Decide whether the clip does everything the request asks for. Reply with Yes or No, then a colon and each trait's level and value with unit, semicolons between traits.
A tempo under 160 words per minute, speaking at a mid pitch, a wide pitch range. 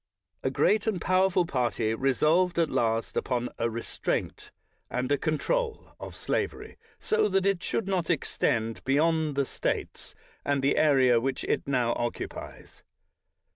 Yes: average, 140 wpm; medium, 145 Hz; wide, 6.7 semitones